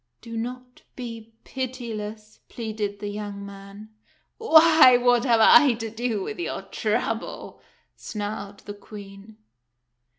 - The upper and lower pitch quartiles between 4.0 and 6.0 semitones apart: No, average, 3.1 semitones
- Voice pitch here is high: Yes, high, 220 Hz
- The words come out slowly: Yes, slow, 130 wpm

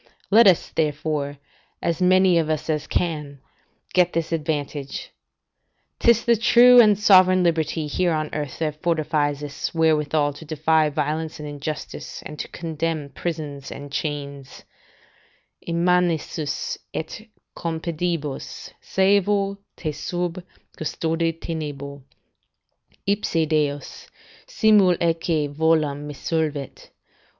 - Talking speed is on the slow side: Yes, slow, 115 wpm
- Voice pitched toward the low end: No, medium, 160 Hz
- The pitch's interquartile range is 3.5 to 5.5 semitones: No, average, 2.9 semitones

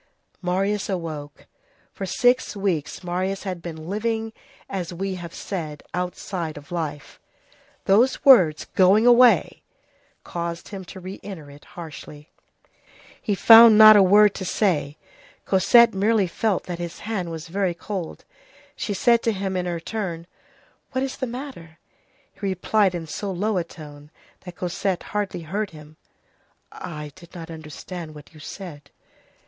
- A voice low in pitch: No, medium, 185 Hz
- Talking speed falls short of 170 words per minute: Yes, average, 150 wpm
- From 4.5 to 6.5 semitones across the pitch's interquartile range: No, average, 3.9 semitones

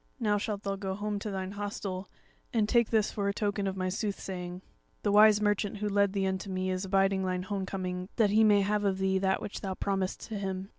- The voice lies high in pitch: Yes, high, 195 Hz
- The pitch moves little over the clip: Yes, narrow, 1.5 semitones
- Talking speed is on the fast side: Yes, fast, 235 wpm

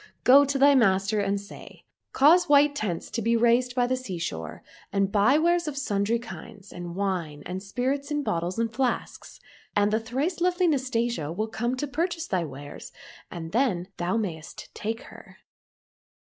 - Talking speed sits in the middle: Yes, average, 175 wpm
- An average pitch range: No, wide, 6.3 semitones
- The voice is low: No, high, 230 Hz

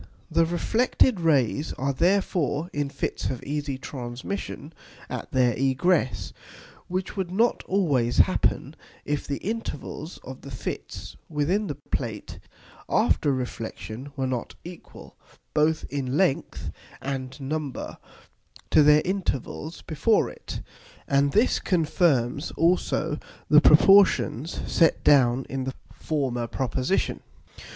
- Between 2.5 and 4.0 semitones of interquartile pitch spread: No, average, 4.7 semitones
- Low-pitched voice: No, medium, 145 Hz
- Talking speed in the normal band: No, slow, 115 wpm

